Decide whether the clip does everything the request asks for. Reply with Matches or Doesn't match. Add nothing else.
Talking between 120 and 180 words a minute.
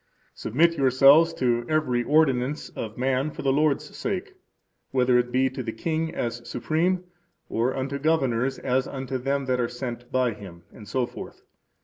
Matches